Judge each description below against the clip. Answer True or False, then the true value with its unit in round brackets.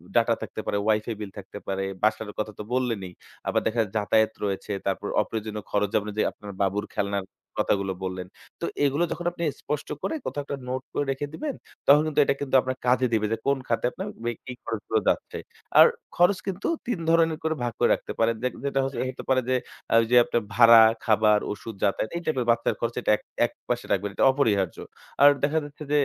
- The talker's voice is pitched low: True (115 Hz)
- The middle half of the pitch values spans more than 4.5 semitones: True (5.2 semitones)